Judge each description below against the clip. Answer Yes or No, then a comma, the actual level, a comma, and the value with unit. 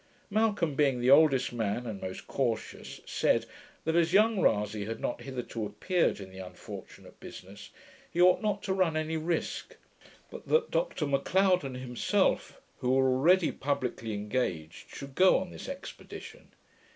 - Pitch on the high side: No, medium, 140 Hz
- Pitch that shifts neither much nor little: No, wide, 8.0 semitones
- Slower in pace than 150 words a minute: No, average, 155 wpm